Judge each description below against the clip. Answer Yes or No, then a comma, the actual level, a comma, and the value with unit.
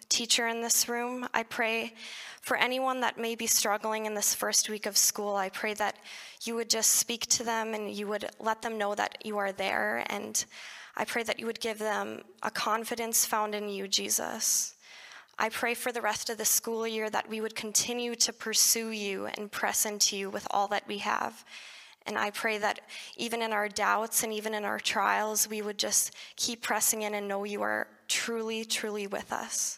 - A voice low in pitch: No, high, 220 Hz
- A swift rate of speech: Yes, fast, 210 wpm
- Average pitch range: No, narrow, 1.7 semitones